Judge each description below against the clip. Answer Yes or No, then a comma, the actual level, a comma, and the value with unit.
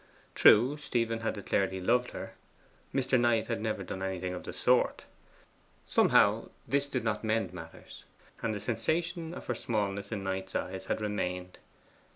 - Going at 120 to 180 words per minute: Yes, average, 165 wpm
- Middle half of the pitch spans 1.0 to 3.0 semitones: No, average, 4.1 semitones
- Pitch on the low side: Yes, low, 110 Hz